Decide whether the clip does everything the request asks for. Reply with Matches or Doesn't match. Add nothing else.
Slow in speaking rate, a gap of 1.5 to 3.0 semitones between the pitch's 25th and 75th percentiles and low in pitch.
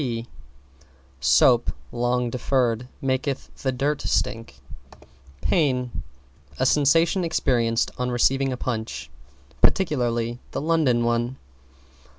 Matches